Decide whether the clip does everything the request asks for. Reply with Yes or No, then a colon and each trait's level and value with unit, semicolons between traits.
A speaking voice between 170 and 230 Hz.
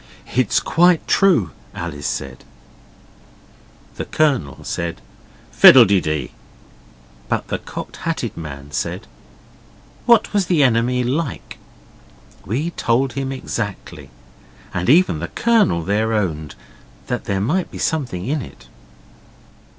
No: low, 115 Hz